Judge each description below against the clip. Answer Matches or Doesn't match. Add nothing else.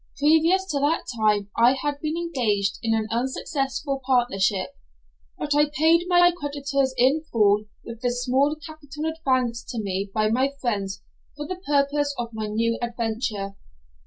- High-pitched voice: Matches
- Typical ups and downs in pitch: Matches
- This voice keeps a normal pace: Matches